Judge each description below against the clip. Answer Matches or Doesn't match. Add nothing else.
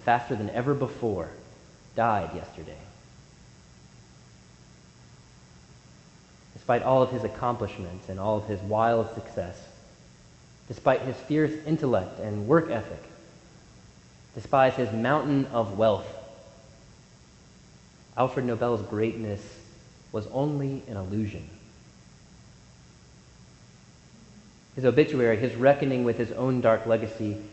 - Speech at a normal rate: Doesn't match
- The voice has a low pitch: Matches